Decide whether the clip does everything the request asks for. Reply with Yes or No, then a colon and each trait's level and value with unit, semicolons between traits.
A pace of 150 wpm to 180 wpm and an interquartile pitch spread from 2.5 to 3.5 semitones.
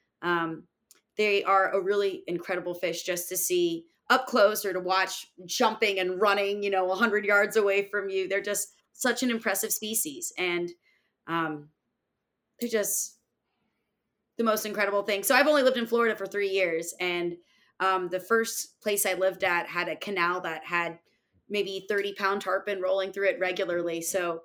Yes: average, 170 wpm; average, 2.9 semitones